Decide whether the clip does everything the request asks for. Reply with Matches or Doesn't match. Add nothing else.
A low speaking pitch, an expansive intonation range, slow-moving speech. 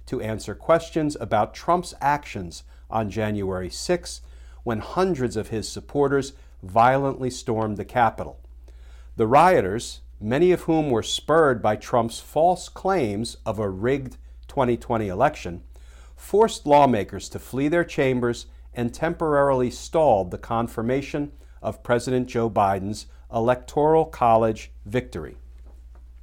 Matches